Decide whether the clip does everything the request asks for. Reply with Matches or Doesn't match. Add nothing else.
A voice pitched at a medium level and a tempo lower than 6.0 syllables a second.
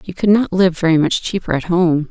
Matches